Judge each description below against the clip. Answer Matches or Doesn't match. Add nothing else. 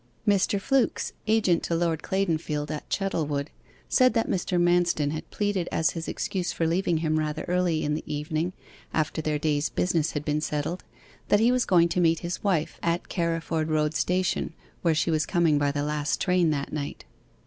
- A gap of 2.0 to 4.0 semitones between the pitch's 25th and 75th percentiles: Matches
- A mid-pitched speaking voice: Matches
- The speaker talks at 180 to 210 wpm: Matches